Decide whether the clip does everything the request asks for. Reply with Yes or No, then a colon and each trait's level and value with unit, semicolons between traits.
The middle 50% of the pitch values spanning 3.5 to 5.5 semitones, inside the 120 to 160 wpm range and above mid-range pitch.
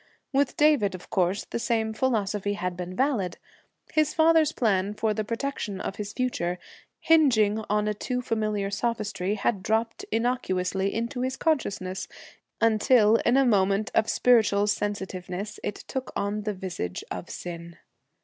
Yes: average, 3.8 semitones; average, 150 wpm; high, 210 Hz